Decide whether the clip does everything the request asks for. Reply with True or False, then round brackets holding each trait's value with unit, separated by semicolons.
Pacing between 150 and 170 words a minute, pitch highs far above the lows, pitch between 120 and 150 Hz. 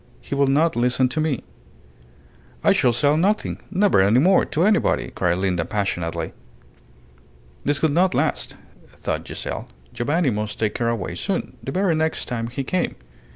True (160 wpm; 7.4 semitones; 135 Hz)